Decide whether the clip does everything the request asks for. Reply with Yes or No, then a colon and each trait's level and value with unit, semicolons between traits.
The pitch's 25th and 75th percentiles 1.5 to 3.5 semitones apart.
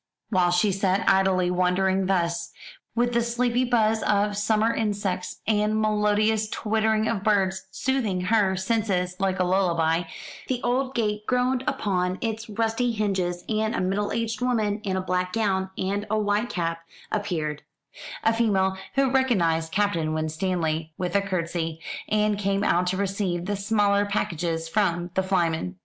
Yes: average, 3.2 semitones